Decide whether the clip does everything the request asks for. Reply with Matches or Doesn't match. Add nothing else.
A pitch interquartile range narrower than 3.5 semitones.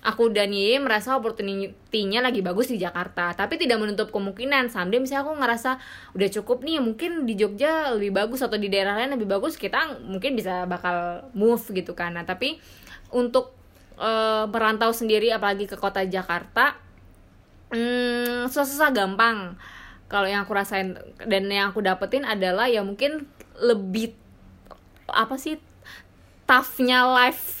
Doesn't match